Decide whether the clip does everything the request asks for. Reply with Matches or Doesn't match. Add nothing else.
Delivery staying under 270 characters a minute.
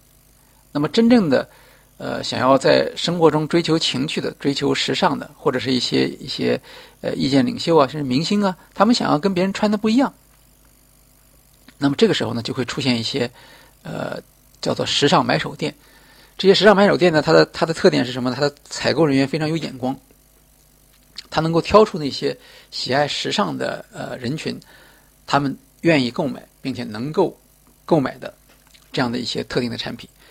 Doesn't match